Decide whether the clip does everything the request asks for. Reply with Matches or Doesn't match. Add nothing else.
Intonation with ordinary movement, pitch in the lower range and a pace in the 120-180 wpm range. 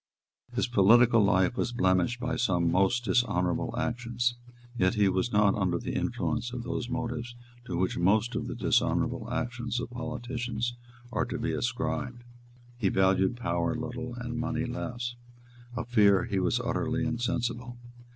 Matches